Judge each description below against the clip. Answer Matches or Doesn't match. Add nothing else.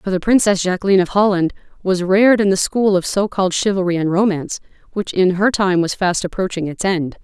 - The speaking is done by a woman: Matches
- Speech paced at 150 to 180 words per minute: Doesn't match